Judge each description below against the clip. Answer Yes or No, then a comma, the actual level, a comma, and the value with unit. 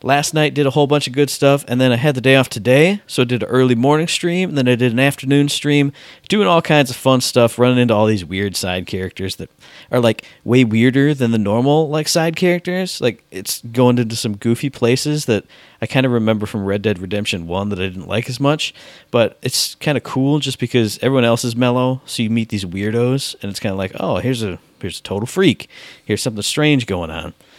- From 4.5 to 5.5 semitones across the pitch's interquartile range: Yes, average, 4.9 semitones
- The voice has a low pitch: Yes, low, 125 Hz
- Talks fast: Yes, fast, 240 wpm